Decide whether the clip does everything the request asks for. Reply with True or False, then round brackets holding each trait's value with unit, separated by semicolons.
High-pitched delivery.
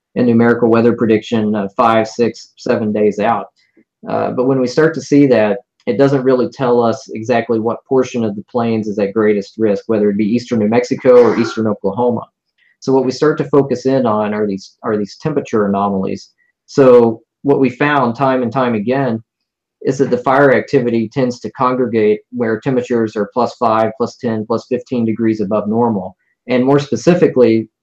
False (120 Hz)